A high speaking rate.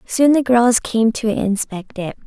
No: average, 185 wpm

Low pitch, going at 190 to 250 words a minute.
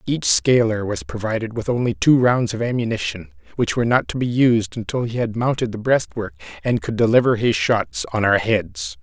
Yes: low, 115 Hz; average, 200 wpm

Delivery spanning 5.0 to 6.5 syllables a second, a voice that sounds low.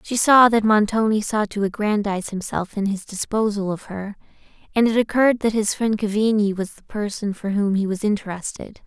No: 5.4 syllables/s; high, 210 Hz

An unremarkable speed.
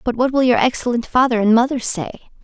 No: fast, 220 wpm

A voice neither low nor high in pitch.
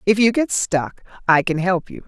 No: high, 195 Hz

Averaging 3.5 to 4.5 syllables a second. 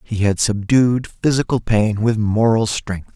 Yes: 4.0 syllables/s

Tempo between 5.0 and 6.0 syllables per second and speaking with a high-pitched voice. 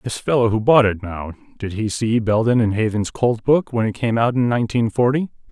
No: 5.4 syllables/s; low, 115 Hz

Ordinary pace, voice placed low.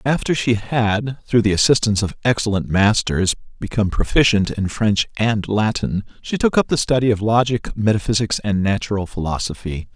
Yes: average, 155 wpm; low, 110 Hz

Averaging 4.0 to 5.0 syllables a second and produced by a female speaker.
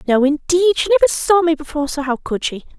No: 6.3 syllables/s; female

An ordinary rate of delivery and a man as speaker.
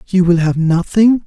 Yes: average, 190 wpm; male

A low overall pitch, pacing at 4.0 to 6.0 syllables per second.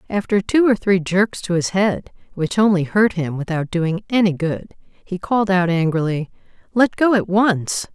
No: high, 190 Hz; 4.5 syllables/s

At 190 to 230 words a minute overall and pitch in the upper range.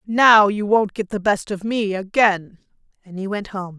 Yes: fast, 205 wpm; high, 205 Hz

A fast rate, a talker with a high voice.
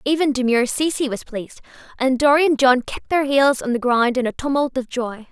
Yes: fast, 225 wpm; very high, 260 Hz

